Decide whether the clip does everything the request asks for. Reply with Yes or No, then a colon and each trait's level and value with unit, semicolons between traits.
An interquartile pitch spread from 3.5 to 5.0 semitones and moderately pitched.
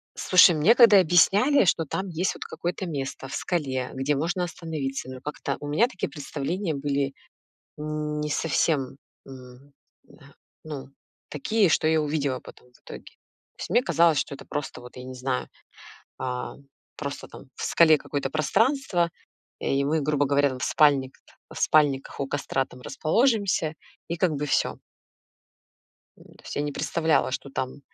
Yes: average, 3.8 semitones; medium, 150 Hz